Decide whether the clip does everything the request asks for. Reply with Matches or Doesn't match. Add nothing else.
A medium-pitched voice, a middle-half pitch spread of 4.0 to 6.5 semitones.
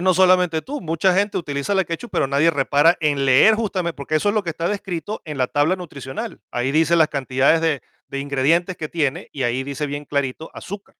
Matches